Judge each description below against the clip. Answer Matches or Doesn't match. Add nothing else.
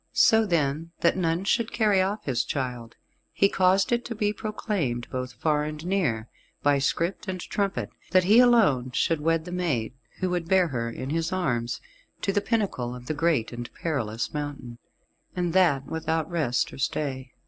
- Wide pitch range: Matches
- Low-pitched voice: Doesn't match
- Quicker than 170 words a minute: Matches